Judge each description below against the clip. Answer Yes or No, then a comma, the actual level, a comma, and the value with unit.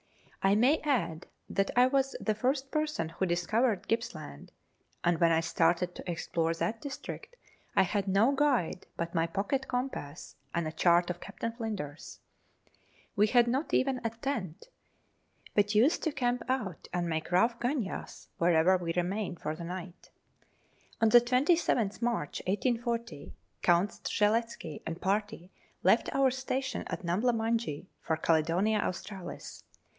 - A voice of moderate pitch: No, high, 205 Hz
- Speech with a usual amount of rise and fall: No, wide, 6.0 semitones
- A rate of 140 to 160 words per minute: Yes, average, 150 wpm